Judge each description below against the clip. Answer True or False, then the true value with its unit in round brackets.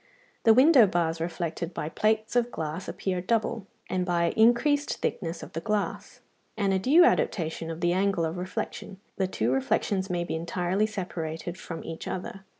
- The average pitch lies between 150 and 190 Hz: True (185 Hz)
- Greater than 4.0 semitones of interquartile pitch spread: True (4.4 semitones)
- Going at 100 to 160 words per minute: False (170 wpm)